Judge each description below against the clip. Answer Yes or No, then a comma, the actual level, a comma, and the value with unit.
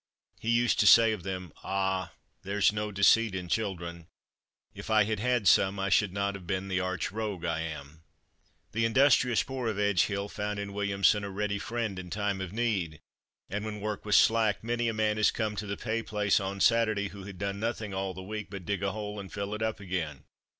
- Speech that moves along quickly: Yes, fast, 220 wpm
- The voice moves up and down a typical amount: No, narrow, 2.2 semitones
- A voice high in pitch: No, low, 100 Hz